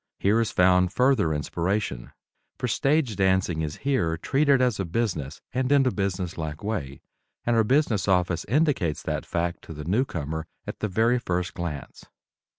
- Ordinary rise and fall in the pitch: No, wide, 6.7 semitones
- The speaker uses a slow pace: No, average, 165 wpm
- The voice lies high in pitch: No, very low, 95 Hz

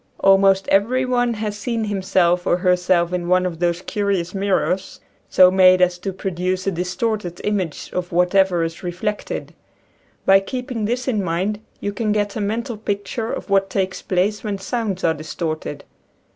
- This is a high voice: Yes, high, 195 Hz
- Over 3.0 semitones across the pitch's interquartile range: No, narrow, 2.6 semitones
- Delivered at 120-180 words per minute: Yes, average, 165 wpm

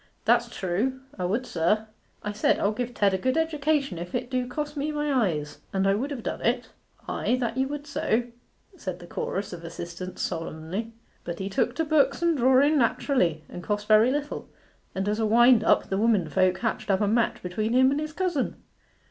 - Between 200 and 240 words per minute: Yes, fast, 205 wpm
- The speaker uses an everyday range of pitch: No, wide, 6.2 semitones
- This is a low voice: No, high, 225 Hz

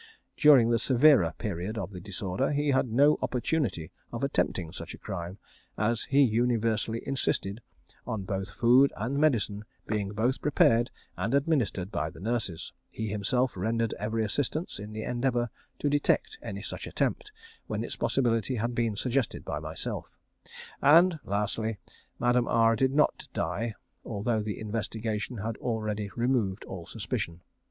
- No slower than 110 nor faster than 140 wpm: No, average, 150 wpm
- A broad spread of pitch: No, average, 3.6 semitones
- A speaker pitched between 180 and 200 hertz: No, low, 115 Hz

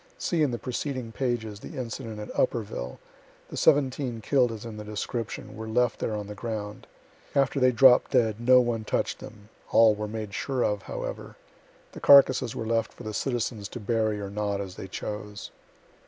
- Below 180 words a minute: No, average, 185 wpm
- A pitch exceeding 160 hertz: No, low, 115 Hz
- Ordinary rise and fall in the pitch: Yes, average, 3.0 semitones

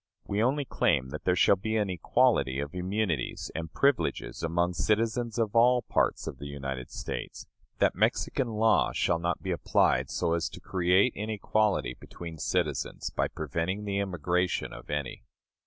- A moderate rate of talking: Yes, average, 160 wpm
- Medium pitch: No, very low, 90 Hz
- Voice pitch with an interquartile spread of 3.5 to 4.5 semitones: No, average, 5.1 semitones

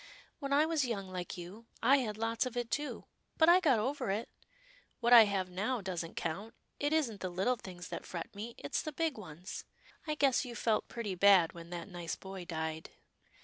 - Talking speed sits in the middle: No, fast, 215 wpm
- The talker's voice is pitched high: Yes, high, 215 Hz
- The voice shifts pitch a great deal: Yes, wide, 5.8 semitones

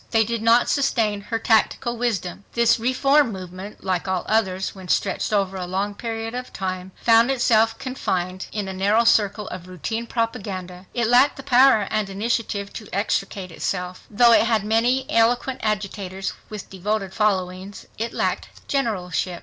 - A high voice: Yes, high, 215 Hz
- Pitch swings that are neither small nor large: Yes, average, 3.5 semitones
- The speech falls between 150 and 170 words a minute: Yes, average, 160 wpm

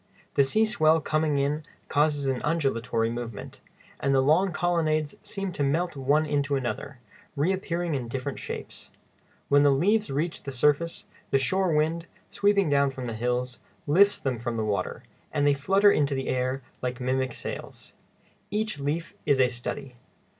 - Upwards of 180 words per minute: No, average, 165 wpm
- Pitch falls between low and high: Yes, medium, 145 Hz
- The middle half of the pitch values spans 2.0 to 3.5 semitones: No, average, 4.1 semitones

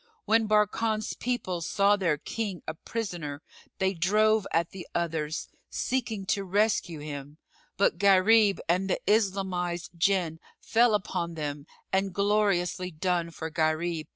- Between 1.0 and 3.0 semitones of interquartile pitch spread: No, average, 3.8 semitones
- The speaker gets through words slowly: Yes, slow, 130 wpm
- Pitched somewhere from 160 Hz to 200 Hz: Yes, medium, 185 Hz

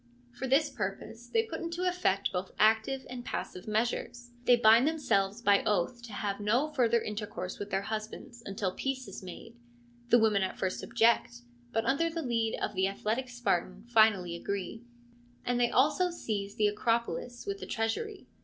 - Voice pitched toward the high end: Yes, high, 225 Hz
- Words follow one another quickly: No, average, 175 wpm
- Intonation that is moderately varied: Yes, average, 4.1 semitones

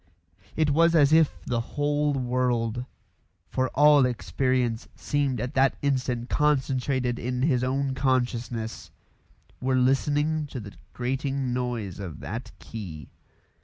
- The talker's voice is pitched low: Yes, low, 130 Hz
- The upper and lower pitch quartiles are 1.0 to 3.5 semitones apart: Yes, narrow, 2.5 semitones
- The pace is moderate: No, slow, 125 wpm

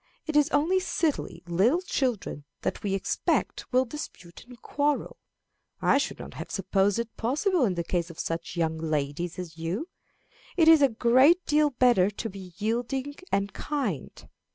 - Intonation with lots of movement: Yes, wide, 8.3 semitones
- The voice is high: Yes, high, 230 Hz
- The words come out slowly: No, average, 165 wpm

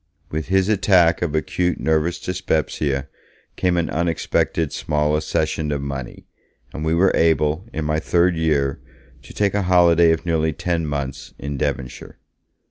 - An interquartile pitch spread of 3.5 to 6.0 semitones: No, average, 2.7 semitones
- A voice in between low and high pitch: No, very low, 80 Hz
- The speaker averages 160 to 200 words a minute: No, average, 150 wpm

